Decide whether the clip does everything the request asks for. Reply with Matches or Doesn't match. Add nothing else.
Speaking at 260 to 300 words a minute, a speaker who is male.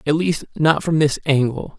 Doesn't match